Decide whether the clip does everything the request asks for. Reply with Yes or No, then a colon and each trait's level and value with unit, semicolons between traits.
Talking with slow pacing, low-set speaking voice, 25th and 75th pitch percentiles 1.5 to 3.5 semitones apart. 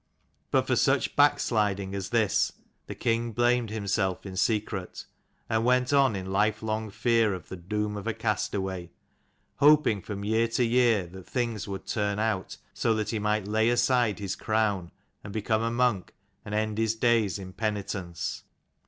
No: average, 170 wpm; low, 105 Hz; average, 2.8 semitones